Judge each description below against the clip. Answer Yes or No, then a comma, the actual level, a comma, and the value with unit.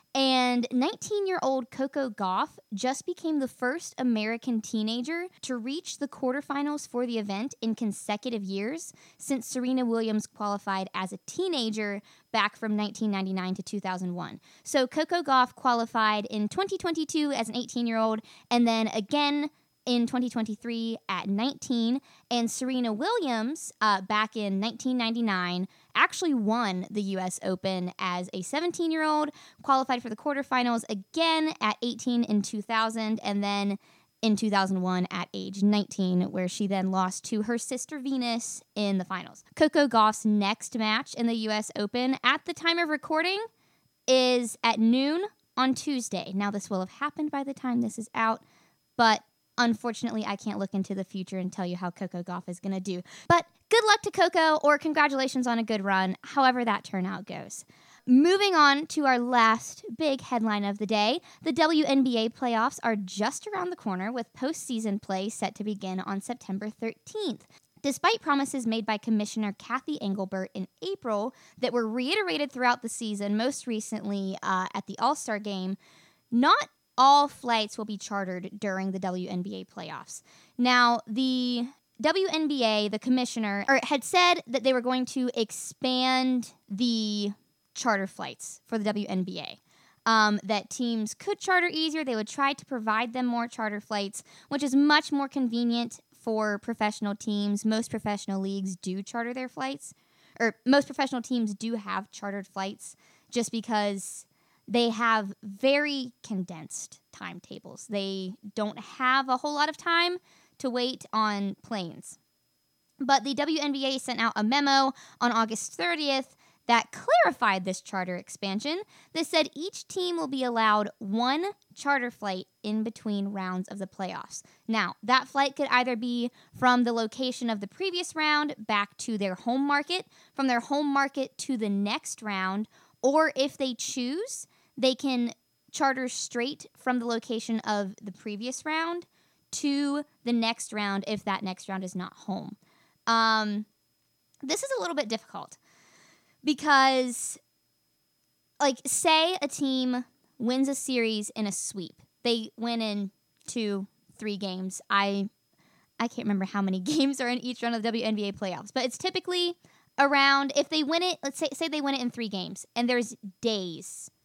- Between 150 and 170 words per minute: Yes, average, 160 wpm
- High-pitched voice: Yes, high, 235 Hz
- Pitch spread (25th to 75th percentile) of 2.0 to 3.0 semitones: No, average, 4.9 semitones